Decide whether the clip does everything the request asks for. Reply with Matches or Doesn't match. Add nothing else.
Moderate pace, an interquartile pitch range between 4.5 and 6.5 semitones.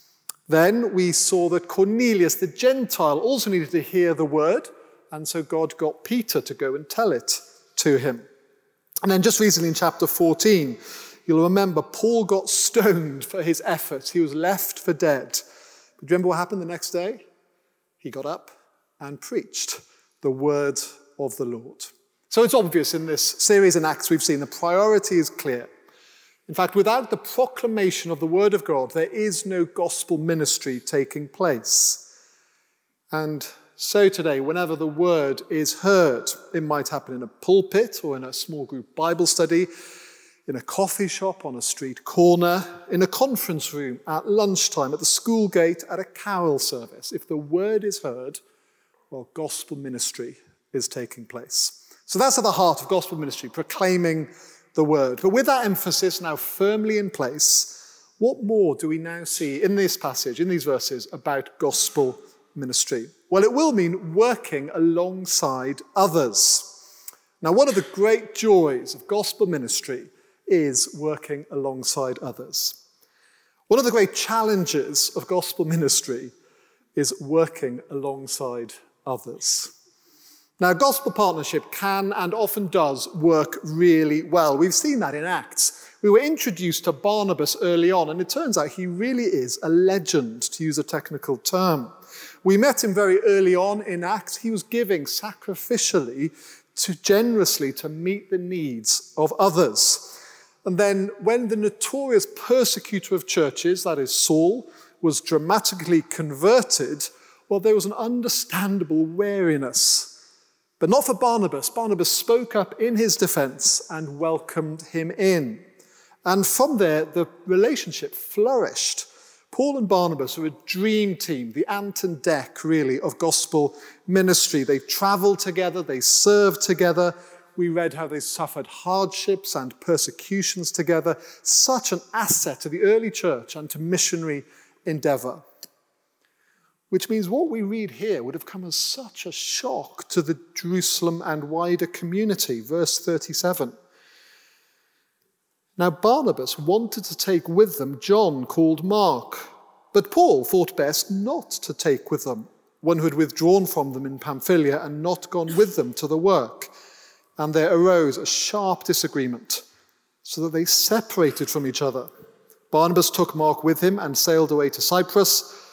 Matches